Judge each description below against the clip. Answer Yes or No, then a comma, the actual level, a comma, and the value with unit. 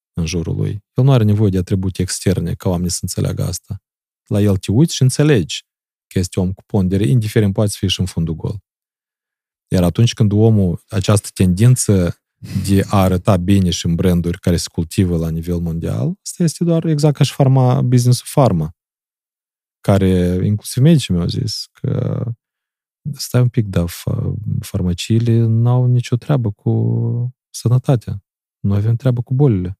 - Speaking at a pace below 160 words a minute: No, average, 165 wpm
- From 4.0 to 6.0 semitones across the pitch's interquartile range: Yes, average, 5.2 semitones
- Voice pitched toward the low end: Yes, low, 110 Hz